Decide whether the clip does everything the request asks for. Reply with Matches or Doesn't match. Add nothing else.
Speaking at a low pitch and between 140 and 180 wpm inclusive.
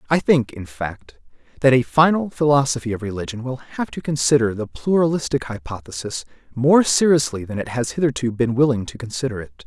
Matches